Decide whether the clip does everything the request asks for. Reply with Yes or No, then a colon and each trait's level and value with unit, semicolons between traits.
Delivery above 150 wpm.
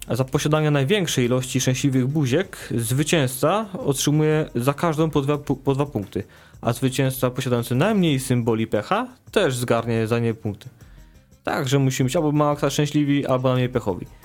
No: average, 145 wpm